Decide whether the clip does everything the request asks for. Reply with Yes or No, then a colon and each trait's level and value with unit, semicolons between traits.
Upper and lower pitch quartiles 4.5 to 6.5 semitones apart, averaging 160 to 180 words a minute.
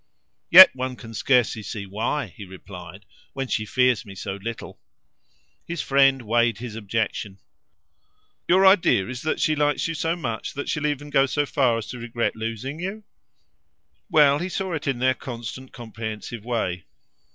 Yes: average, 4.8 semitones; average, 165 wpm